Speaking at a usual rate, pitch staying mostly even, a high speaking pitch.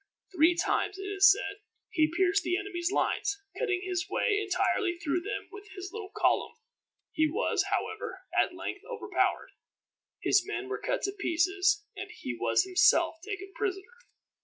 Yes: average, 160 wpm; narrow, 2.2 semitones; very high, 390 Hz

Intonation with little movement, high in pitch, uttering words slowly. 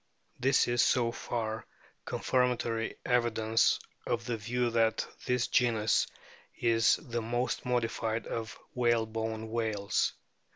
No: narrow, 1.4 semitones; low, 115 Hz; slow, 110 wpm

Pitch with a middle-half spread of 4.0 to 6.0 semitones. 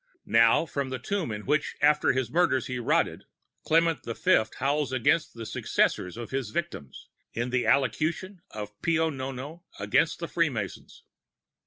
Yes: average, 5.2 semitones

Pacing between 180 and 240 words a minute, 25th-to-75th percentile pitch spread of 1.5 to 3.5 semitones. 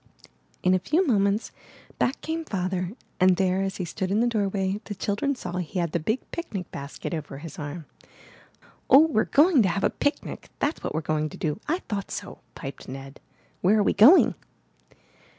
No: average, 195 wpm; average, 5.1 semitones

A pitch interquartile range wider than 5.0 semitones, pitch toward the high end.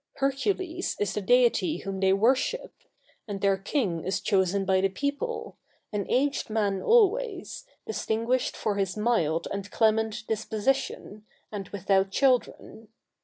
Yes: wide, 5.6 semitones; high, 220 Hz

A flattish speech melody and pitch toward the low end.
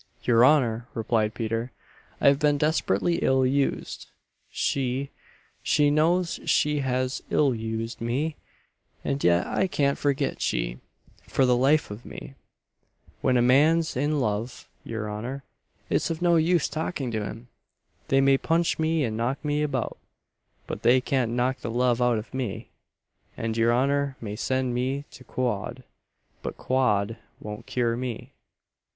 No: average, 3.6 semitones; low, 130 Hz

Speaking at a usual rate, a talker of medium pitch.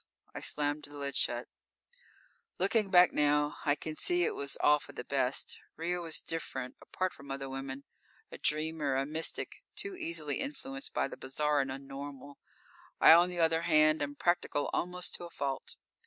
Yes: average, 180 wpm; medium, 150 Hz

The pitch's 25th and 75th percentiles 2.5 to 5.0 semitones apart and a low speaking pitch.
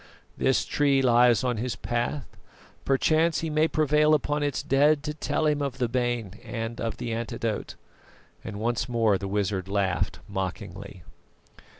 No: wide, 5.4 semitones; low, 120 Hz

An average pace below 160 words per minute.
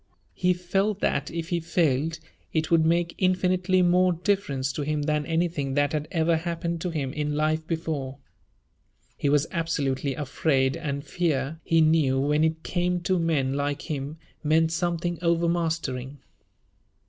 Yes: average, 150 wpm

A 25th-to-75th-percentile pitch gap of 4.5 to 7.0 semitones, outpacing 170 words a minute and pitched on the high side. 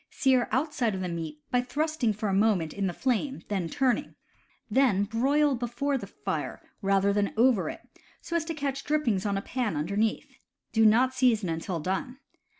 Yes: average, 5.2 semitones; average, 180 wpm; high, 225 Hz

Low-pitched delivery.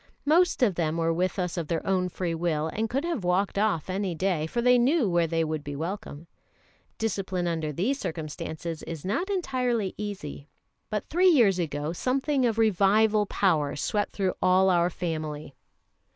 No: medium, 185 Hz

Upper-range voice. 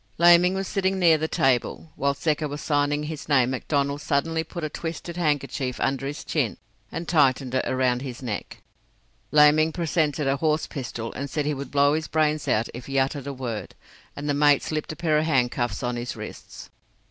No: medium, 145 Hz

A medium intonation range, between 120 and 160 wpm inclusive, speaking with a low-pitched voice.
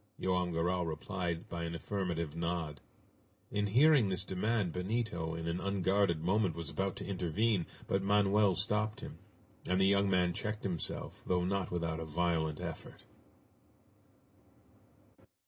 Yes: average, 3.1 semitones; average, 140 wpm; very low, 90 Hz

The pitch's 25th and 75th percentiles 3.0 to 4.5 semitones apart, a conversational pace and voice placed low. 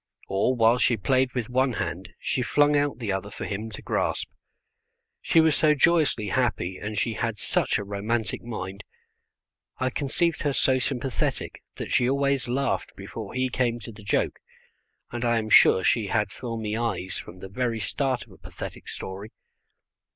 Yes: average, 3.8 semitones; average, 175 wpm; low, 120 Hz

